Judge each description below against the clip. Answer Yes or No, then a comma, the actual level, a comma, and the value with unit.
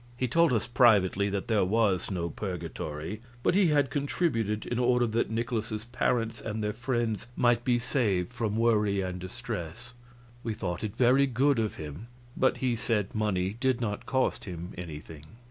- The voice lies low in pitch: Yes, low, 110 Hz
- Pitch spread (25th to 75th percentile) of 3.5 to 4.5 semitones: Yes, average, 3.9 semitones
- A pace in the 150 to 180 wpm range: Yes, average, 170 wpm